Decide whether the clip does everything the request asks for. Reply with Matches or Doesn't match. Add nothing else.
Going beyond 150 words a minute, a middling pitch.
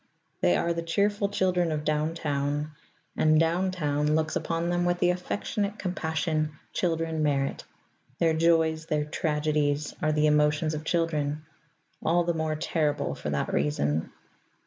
Doesn't match